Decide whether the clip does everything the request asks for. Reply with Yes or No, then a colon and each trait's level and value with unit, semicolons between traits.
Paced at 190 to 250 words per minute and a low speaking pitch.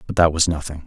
No: fast, 280 wpm; very low, 80 Hz